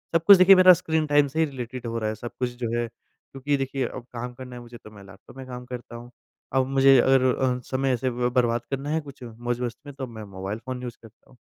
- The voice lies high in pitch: No, low, 125 Hz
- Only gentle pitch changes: Yes, narrow, 2.3 semitones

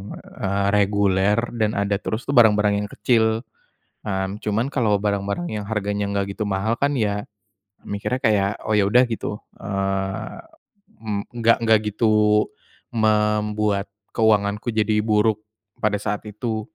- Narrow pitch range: Yes, narrow, 1.5 semitones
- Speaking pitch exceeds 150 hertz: No, low, 105 Hz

